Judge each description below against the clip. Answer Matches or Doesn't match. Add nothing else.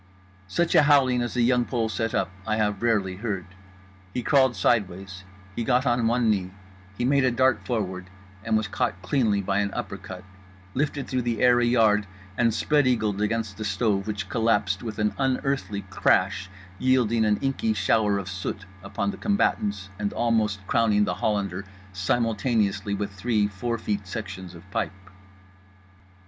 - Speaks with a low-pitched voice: Matches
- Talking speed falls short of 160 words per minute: Doesn't match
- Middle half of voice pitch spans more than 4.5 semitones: Doesn't match